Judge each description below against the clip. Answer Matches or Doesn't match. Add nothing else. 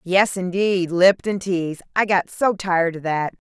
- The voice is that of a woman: Matches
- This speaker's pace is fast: Doesn't match